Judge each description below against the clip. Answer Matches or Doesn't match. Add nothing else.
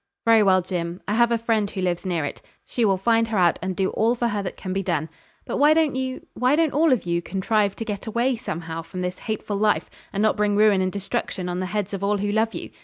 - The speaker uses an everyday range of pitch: Matches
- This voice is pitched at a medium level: Doesn't match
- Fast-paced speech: Matches